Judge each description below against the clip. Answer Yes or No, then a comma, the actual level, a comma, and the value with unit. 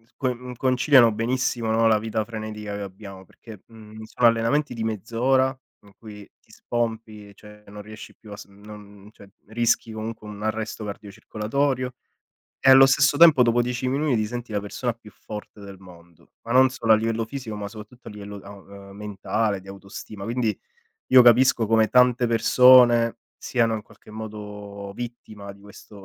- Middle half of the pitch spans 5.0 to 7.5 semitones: No, average, 2.7 semitones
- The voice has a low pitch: Yes, low, 110 Hz